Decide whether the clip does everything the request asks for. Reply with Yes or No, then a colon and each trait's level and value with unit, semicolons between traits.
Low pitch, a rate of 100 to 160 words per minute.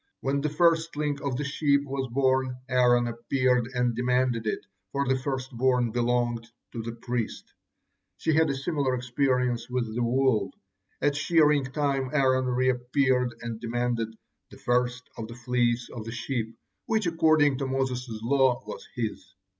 Yes: low, 125 Hz; average, 155 wpm